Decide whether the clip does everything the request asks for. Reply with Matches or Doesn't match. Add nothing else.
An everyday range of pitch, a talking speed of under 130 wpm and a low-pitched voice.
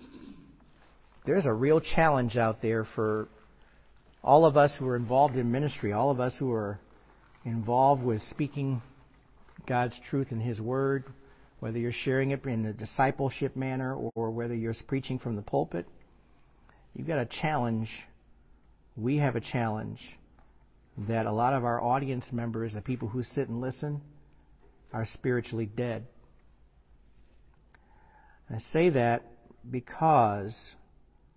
Doesn't match